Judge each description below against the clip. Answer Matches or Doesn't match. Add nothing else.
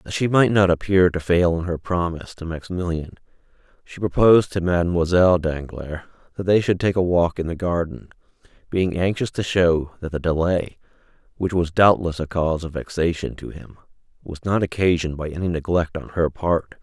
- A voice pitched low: Matches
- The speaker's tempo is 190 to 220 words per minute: Doesn't match